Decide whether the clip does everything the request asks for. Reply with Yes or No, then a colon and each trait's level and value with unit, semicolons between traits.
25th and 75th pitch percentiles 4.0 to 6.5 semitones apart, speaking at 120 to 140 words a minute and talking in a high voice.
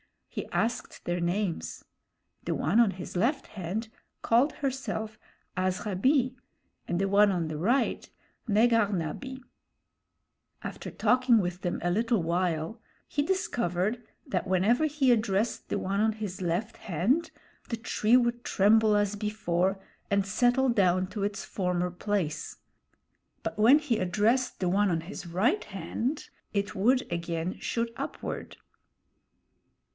Yes: average, 4.6 semitones; slow, 135 wpm; high, 205 Hz